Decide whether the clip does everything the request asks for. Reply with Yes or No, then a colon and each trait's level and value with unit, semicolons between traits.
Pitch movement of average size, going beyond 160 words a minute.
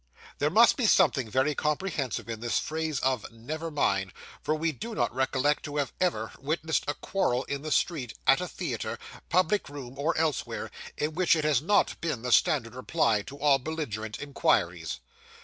Yes: average, 3.9 semitones; average, 180 wpm